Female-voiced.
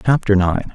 No: male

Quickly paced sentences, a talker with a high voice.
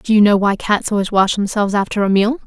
Yes: fast, 270 wpm; high, 205 Hz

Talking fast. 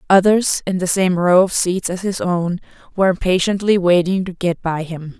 No: average, 195 wpm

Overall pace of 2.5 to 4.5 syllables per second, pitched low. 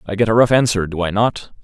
No: 6.2 syllables/s; low, 105 Hz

